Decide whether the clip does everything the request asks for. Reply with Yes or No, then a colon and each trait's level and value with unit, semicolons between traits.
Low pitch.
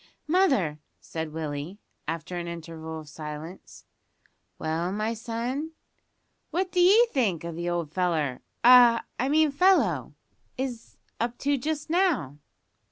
No: high, 200 Hz